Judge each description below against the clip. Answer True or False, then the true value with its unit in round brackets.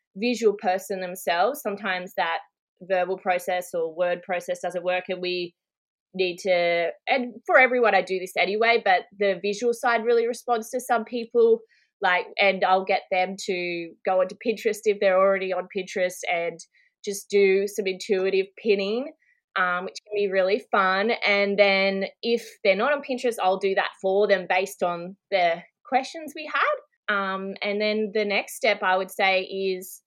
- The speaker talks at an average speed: True (170 wpm)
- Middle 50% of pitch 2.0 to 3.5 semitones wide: True (3.2 semitones)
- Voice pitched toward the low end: False (195 Hz)